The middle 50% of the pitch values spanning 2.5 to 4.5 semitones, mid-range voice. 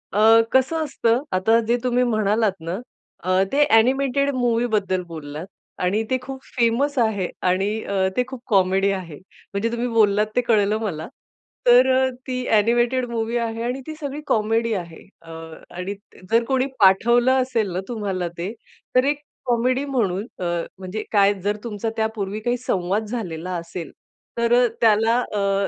No: average, 3.9 semitones; high, 220 Hz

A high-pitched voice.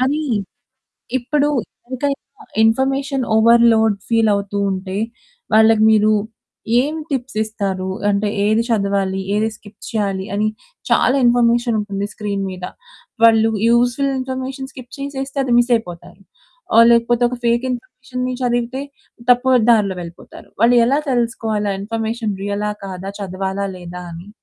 Yes: high, 225 Hz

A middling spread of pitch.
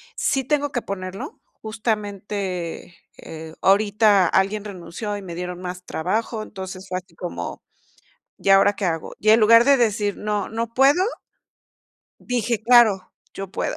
Yes: average, 3.2 semitones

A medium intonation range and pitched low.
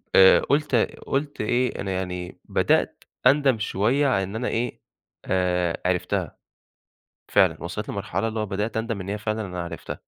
Yes: average, 4.5 semitones; low, 105 Hz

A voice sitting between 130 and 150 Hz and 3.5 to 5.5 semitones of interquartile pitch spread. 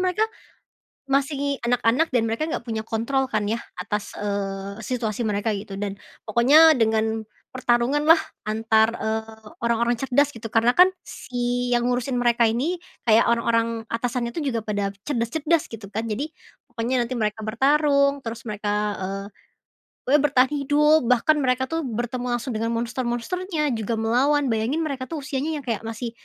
No: high, 240 Hz; average, 3.8 semitones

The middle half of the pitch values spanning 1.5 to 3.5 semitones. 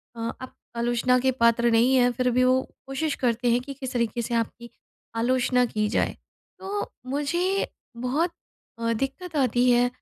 Yes: narrow, 2.4 semitones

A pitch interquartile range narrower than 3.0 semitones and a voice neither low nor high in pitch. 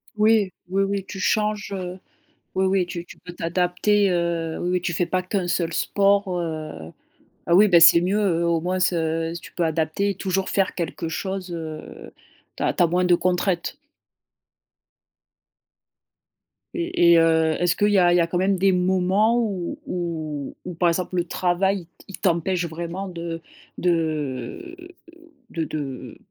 Yes: narrow, 2.4 semitones; medium, 180 Hz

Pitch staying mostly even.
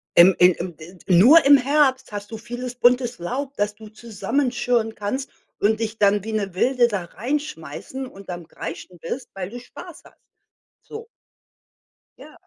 No: average, 4.8 semitones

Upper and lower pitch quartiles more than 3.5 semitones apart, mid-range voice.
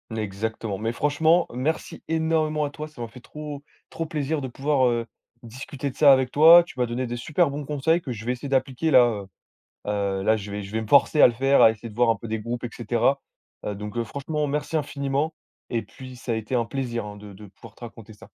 No: average, 4.6 semitones; low, 125 Hz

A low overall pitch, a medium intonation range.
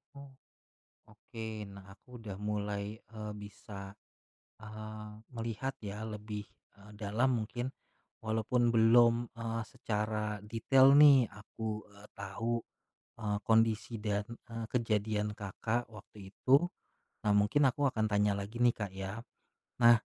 No: low, 110 Hz; narrow, 2.1 semitones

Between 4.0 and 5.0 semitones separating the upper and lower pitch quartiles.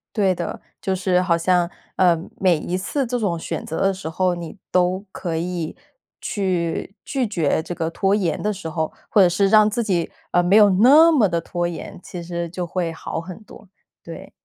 No: average, 2.7 semitones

